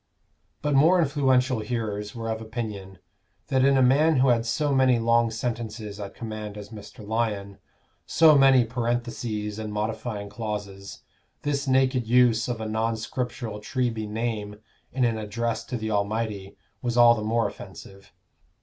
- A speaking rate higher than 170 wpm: No, average, 155 wpm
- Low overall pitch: Yes, low, 115 Hz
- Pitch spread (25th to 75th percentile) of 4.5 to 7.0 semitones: No, average, 2.9 semitones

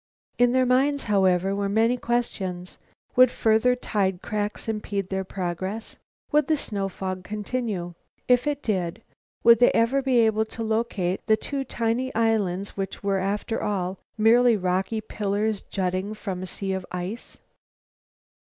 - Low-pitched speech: No, high, 210 Hz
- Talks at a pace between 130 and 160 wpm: Yes, average, 150 wpm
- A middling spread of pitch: Yes, average, 3.6 semitones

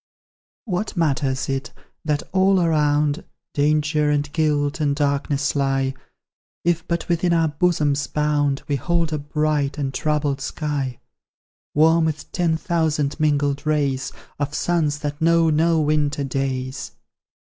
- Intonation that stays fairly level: Yes, narrow, 2.2 semitones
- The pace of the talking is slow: Yes, slow, 125 wpm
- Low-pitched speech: No, medium, 150 Hz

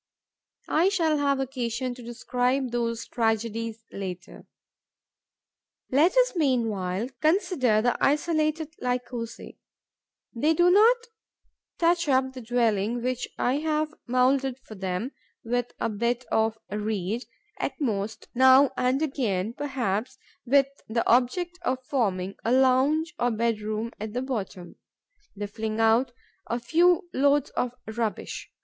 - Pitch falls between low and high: No, very high, 250 Hz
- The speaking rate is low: Yes, slow, 125 wpm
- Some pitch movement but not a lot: Yes, average, 4.2 semitones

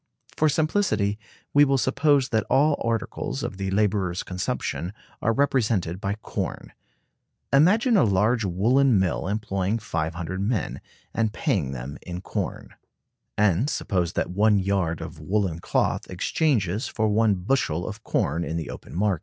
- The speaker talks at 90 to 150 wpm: Yes, average, 145 wpm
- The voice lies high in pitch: No, low, 105 Hz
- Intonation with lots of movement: No, average, 5.0 semitones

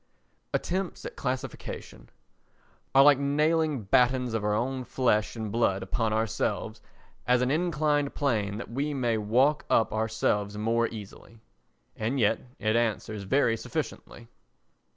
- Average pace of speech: No, slow, 130 wpm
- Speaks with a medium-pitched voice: No, low, 115 Hz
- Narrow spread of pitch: No, average, 4.1 semitones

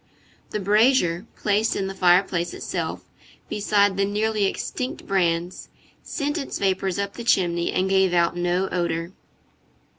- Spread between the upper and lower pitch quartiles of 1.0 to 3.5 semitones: Yes, average, 2.9 semitones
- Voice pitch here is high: Yes, high, 195 Hz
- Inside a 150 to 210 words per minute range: No, average, 140 wpm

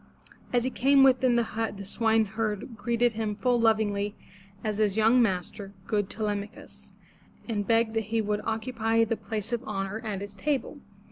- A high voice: Yes, high, 220 Hz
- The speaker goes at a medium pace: Yes, average, 180 wpm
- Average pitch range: No, narrow, 2.0 semitones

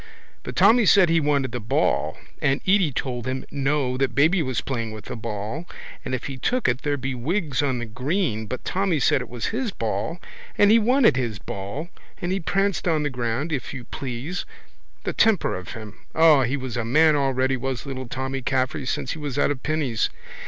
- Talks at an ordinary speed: No, fast, 210 wpm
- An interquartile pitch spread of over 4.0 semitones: Yes, average, 4.6 semitones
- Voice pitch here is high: No, low, 135 Hz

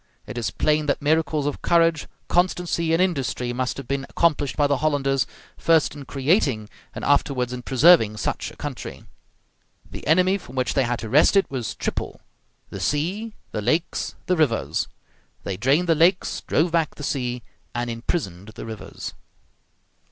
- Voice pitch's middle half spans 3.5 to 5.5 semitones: Yes, average, 4.9 semitones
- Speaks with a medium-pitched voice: Yes, medium, 145 Hz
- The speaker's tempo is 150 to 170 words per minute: Yes, average, 165 wpm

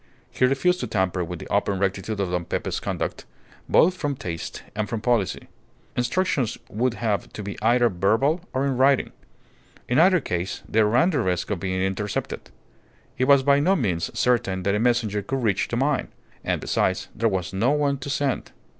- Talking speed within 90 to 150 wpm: No, average, 190 wpm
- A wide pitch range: Yes, wide, 5.8 semitones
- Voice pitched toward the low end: Yes, low, 115 Hz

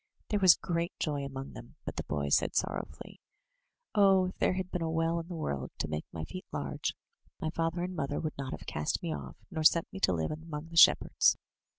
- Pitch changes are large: No, average, 4.6 semitones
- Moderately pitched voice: Yes, medium, 160 Hz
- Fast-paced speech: Yes, fast, 225 wpm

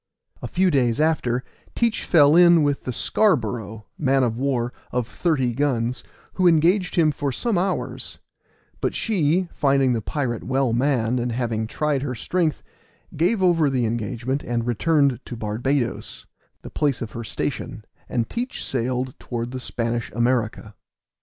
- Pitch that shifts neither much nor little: Yes, average, 4.6 semitones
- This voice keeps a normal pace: Yes, average, 155 wpm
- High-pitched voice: No, low, 130 Hz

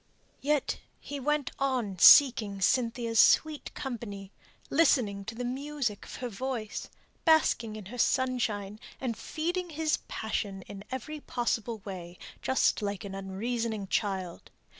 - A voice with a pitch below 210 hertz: No, high, 235 Hz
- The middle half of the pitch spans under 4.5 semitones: No, average, 5.0 semitones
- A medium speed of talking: No, slow, 130 wpm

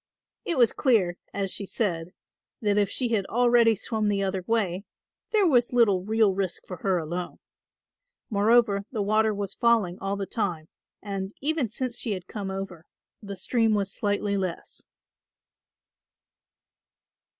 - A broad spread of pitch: No, average, 3.1 semitones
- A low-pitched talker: No, high, 205 Hz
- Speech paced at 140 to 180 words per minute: Yes, average, 150 wpm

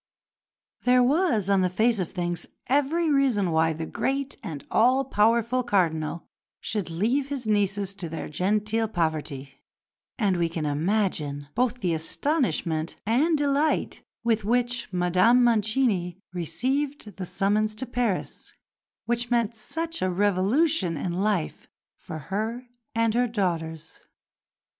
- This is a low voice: No, high, 210 Hz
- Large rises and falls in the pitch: Yes, wide, 6.0 semitones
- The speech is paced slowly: Yes, slow, 130 wpm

